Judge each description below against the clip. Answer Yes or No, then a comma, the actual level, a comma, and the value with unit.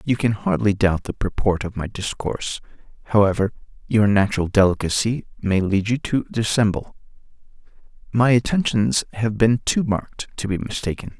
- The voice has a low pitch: Yes, low, 105 Hz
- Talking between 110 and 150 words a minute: Yes, average, 145 wpm